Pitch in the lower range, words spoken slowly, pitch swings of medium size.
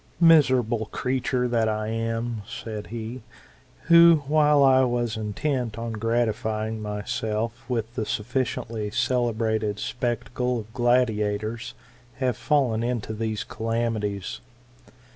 No: low, 115 Hz; slow, 110 wpm; narrow, 2.3 semitones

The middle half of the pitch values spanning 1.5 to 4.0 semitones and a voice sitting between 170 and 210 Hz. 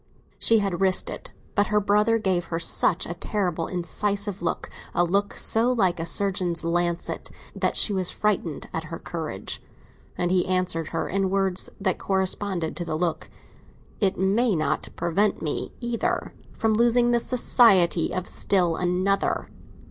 Yes: average, 3.2 semitones; high, 190 Hz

